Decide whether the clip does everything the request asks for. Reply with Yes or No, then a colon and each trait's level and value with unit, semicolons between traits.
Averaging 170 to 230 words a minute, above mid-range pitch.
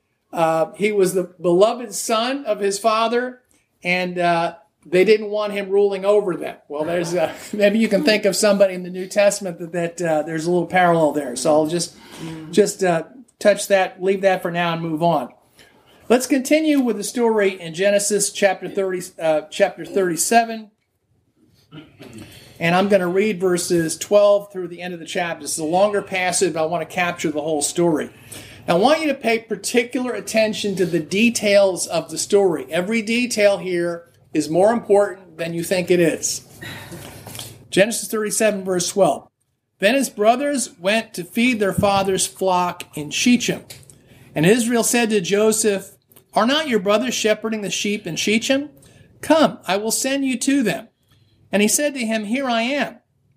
Yes: average, 180 wpm; high, 195 Hz